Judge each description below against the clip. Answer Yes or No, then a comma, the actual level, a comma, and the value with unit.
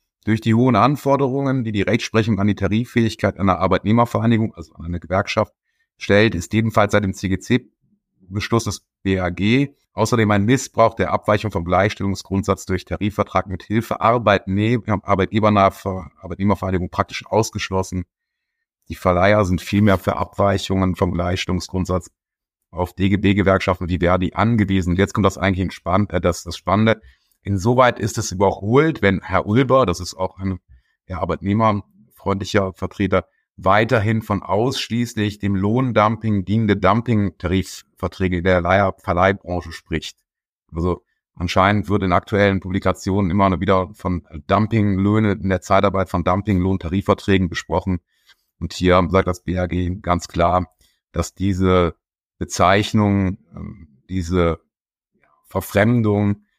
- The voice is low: Yes, low, 100 Hz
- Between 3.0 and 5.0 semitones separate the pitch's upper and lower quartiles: No, narrow, 2.6 semitones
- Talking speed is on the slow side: Yes, slow, 120 wpm